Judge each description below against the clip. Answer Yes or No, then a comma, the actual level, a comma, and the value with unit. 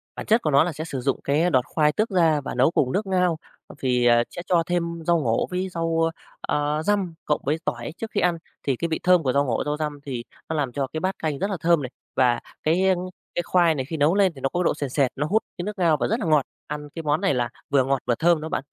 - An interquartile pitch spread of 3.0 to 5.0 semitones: Yes, average, 4.2 semitones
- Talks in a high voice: No, medium, 155 Hz